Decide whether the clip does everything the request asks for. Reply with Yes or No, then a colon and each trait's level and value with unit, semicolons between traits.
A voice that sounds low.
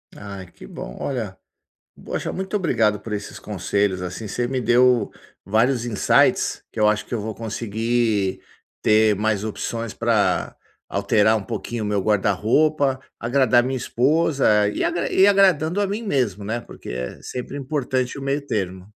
Yes: low, 115 Hz